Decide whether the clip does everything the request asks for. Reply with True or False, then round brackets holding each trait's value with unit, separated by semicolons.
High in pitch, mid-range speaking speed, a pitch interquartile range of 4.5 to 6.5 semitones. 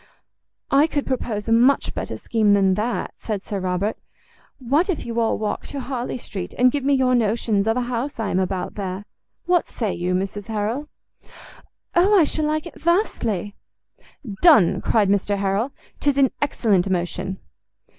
True (225 Hz; 170 wpm; 5.6 semitones)